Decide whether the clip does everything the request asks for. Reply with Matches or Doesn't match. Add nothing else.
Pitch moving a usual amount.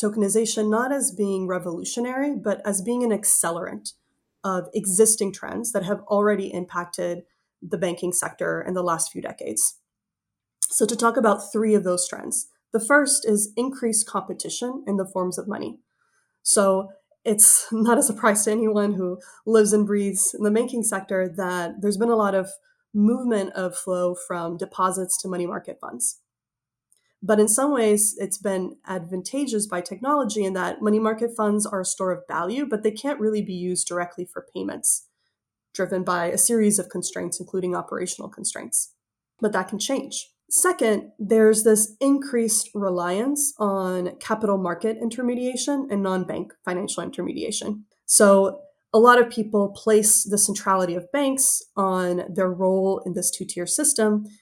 Matches